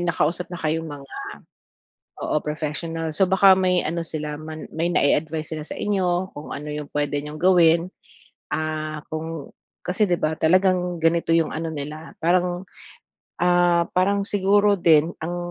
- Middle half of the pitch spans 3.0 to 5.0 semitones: No, narrow, 2.5 semitones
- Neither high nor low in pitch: Yes, medium, 165 Hz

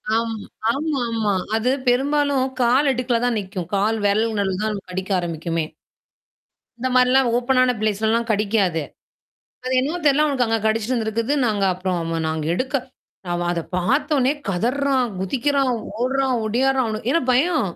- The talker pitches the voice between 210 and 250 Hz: Yes, high, 235 Hz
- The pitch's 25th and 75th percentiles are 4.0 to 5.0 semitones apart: Yes, average, 4.6 semitones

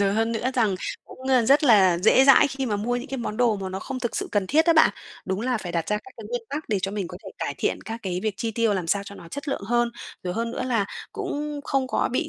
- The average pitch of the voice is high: Yes, high, 230 Hz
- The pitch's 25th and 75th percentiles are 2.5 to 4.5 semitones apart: No, average, 5.0 semitones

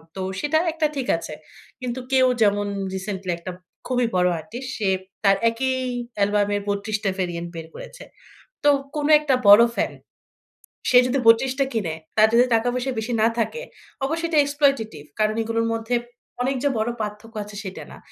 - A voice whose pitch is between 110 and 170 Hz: No, high, 225 Hz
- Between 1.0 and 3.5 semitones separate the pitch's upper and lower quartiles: No, average, 4.2 semitones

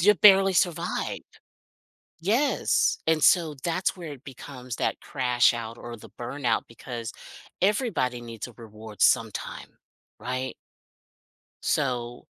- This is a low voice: Yes, low, 130 Hz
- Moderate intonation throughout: No, wide, 6.5 semitones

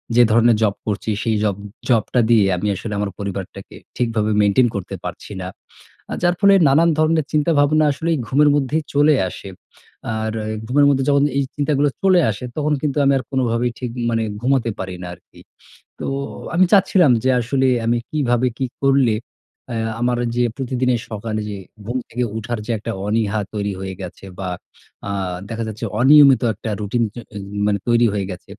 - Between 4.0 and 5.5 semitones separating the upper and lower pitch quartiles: Yes, average, 4.7 semitones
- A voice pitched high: No, low, 120 Hz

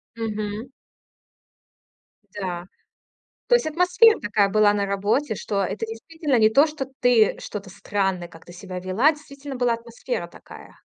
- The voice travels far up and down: Yes, wide, 5.9 semitones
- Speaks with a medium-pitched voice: No, high, 220 Hz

